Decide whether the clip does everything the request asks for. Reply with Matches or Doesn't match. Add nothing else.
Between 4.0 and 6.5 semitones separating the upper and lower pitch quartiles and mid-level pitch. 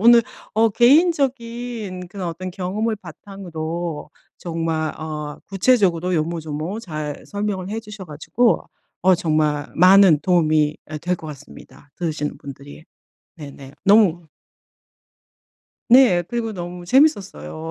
Matches